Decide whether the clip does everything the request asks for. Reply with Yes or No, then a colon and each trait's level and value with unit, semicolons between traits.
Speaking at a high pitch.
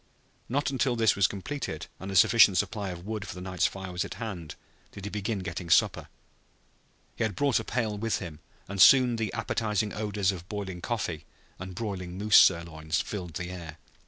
No: low, 100 Hz